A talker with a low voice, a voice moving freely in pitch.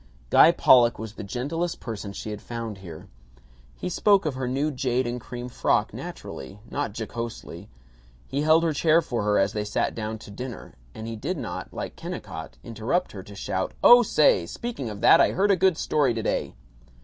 Yes: low, 120 Hz; wide, 6.4 semitones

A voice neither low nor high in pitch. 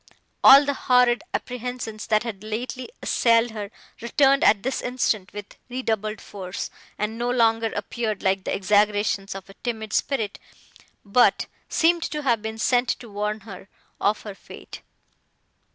No: high, 220 Hz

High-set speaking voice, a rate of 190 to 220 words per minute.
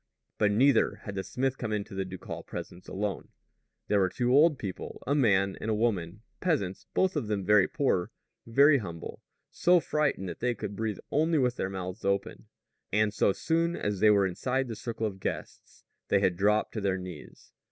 No: low, 105 Hz; average, 195 wpm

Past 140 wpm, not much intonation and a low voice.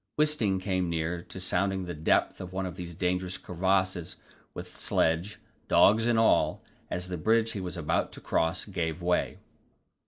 Yes: average, 165 wpm; narrow, 2.0 semitones; very low, 90 Hz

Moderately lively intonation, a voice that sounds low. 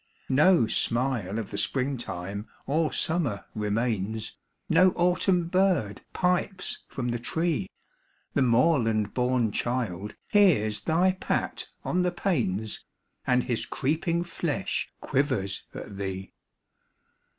No: wide, 8.0 semitones; low, 125 Hz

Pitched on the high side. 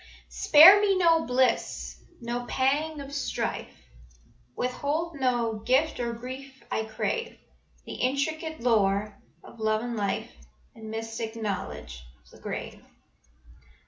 Yes: very high, 250 Hz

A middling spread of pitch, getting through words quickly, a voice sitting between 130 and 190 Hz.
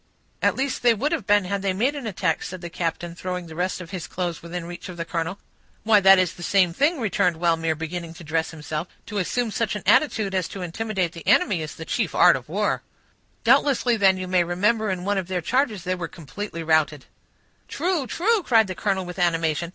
Yes: average, 4.1 semitones; fast, 220 wpm; medium, 185 Hz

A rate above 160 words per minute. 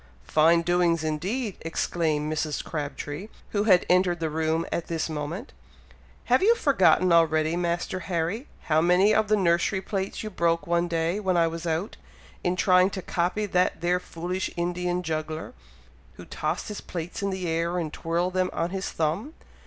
Yes: average, 170 wpm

